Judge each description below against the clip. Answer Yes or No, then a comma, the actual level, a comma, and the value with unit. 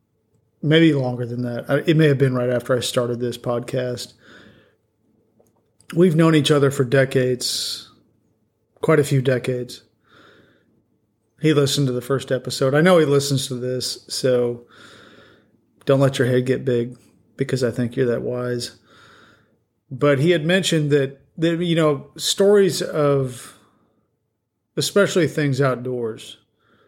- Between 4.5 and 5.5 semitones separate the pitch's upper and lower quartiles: No, average, 3.5 semitones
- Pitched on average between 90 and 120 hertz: No, low, 130 Hz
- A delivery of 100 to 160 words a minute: Yes, average, 140 wpm